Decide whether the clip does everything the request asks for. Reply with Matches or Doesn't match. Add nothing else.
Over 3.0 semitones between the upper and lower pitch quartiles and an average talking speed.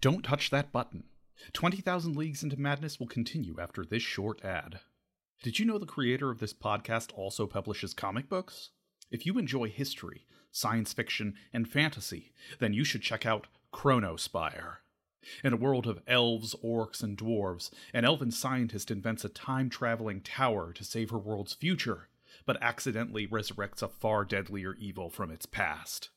Matches